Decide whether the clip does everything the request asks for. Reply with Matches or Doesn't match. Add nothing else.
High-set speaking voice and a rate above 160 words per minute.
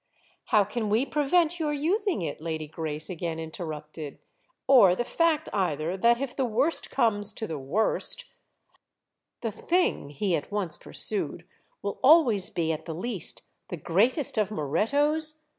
Doesn't match